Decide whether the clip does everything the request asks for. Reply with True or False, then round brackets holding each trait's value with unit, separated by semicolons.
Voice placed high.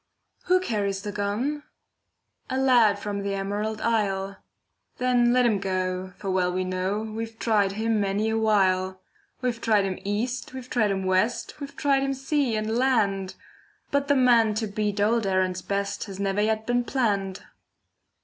True (210 Hz)